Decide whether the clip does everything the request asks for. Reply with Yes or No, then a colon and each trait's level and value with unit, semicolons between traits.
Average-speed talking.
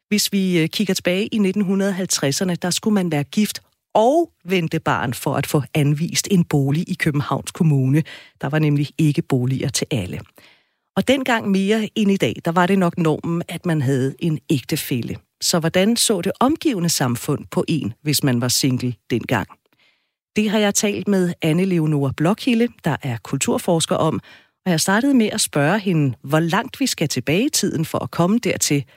Yes: average, 185 wpm